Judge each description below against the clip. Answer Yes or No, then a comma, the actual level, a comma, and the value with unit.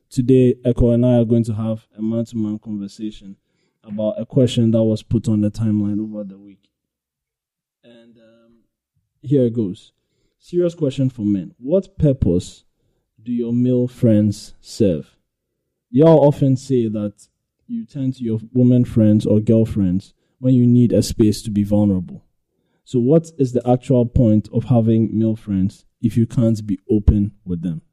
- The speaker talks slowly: No, average, 165 wpm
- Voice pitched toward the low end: Yes, low, 115 Hz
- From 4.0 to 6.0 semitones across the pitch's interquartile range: No, average, 3.0 semitones